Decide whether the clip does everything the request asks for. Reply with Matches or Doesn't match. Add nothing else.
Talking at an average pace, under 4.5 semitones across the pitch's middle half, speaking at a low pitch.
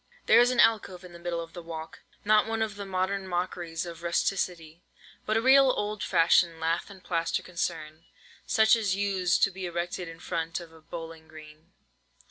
Doesn't match